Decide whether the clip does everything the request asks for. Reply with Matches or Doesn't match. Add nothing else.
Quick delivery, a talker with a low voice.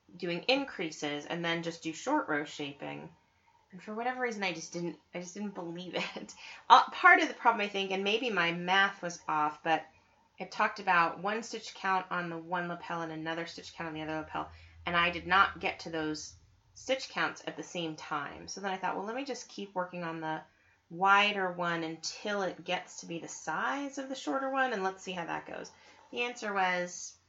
Doesn't match